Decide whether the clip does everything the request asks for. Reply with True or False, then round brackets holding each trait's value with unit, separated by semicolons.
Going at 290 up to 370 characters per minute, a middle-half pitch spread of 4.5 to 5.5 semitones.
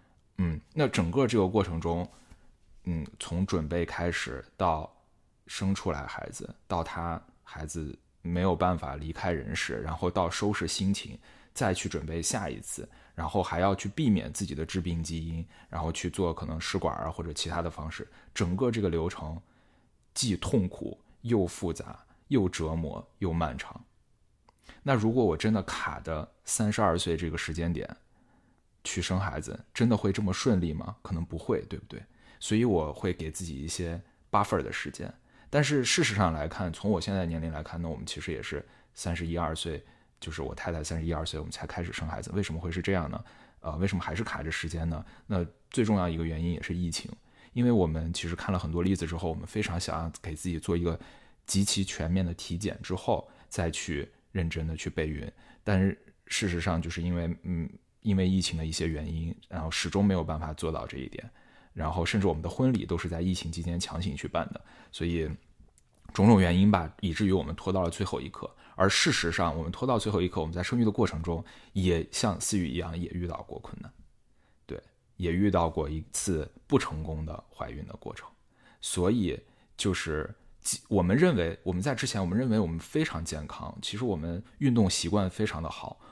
False (295 characters per minute; 3.2 semitones)